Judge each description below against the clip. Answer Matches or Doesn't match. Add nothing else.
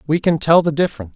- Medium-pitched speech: Matches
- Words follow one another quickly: Matches